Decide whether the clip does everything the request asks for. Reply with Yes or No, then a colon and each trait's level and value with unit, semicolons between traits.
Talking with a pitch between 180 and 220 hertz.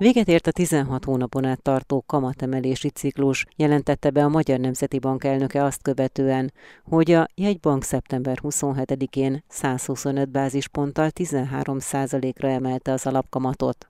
No: low, 135 Hz